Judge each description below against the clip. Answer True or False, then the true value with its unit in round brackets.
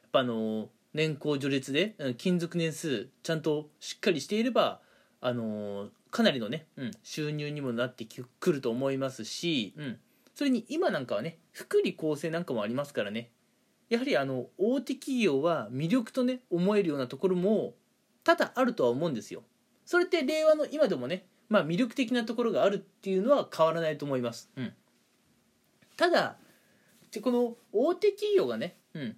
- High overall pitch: False (180 Hz)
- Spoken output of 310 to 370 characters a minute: True (350 characters per minute)